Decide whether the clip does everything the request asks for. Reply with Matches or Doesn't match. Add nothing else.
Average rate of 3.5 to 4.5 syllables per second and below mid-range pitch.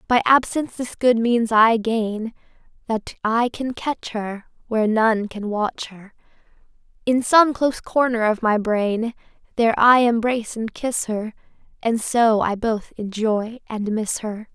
Doesn't match